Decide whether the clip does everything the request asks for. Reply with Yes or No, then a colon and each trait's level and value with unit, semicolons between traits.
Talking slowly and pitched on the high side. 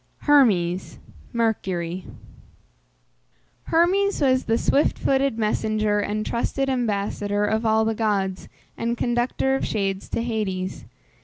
Yes: slow, 110 wpm; high, 220 Hz